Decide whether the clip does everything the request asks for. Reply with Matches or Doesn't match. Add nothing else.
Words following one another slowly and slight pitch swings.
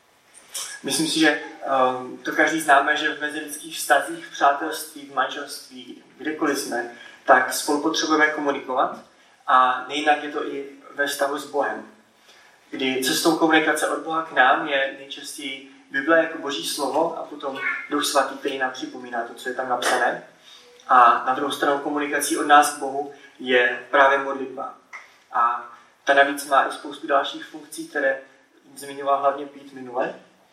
Doesn't match